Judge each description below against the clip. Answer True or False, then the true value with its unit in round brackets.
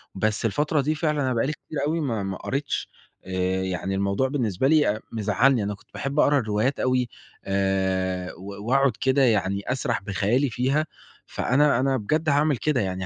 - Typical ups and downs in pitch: False (6.0 semitones)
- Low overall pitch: True (120 Hz)